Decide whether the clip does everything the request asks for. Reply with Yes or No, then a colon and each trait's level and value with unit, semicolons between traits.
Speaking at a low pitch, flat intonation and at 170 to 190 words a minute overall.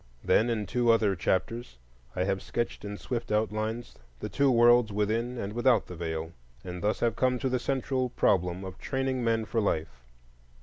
No: low, 110 Hz; average, 3.9 semitones; average, 180 wpm